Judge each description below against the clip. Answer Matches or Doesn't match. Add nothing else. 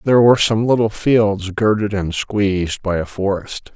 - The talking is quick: Doesn't match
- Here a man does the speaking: Matches